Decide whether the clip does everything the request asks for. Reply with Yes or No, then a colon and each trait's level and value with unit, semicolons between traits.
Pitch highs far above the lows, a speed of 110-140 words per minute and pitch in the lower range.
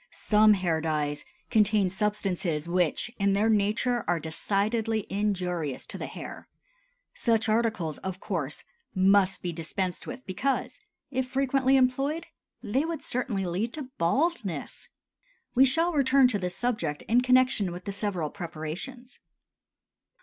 No: wide, 6.0 semitones; slow, 135 wpm; high, 205 Hz